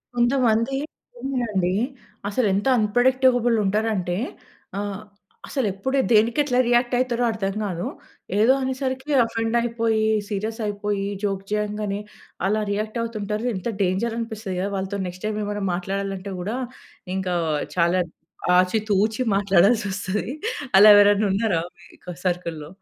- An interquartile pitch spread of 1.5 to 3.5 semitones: Yes, average, 3.2 semitones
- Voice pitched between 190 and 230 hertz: Yes, high, 210 Hz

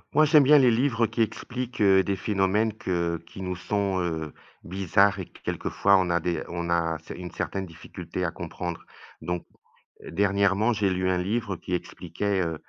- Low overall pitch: Yes, very low, 95 Hz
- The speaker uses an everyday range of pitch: Yes, average, 3.2 semitones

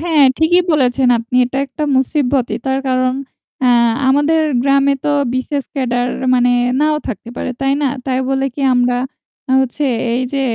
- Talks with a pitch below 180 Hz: No, very high, 265 Hz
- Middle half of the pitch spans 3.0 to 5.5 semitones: No, narrow, 2.4 semitones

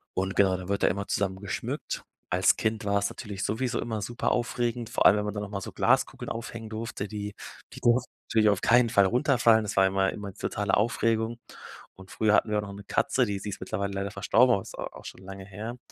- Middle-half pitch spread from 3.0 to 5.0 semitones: No, narrow, 2.6 semitones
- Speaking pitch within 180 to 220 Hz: No, low, 105 Hz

